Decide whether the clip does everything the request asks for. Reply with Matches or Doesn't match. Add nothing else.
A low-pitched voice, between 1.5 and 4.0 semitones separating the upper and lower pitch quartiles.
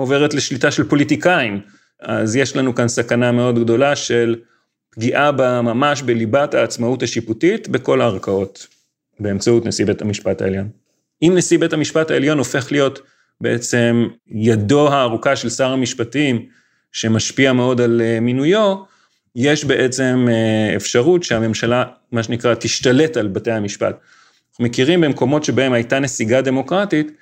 Matches